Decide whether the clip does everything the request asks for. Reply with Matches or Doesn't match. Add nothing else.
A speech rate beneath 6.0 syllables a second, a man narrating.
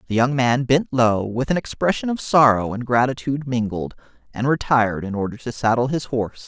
Matches